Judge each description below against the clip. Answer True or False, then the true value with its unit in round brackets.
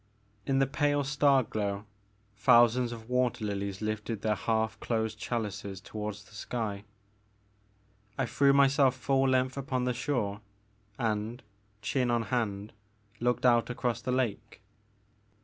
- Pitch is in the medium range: False (120 Hz)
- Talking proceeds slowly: True (130 wpm)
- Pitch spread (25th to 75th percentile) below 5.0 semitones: True (3.2 semitones)